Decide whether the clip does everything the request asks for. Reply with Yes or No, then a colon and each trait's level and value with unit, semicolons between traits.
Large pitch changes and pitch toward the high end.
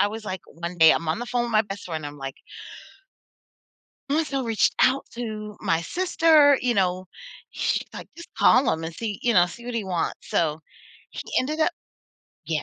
Yes: wide, 6.6 semitones; high, 215 Hz